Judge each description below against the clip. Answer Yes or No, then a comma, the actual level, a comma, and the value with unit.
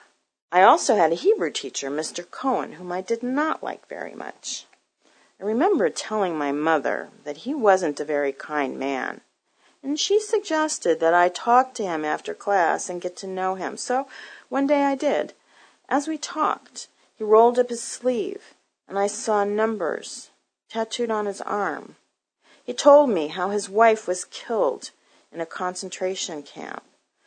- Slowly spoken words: No, average, 165 wpm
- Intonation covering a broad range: Yes, wide, 6.8 semitones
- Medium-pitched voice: No, high, 210 Hz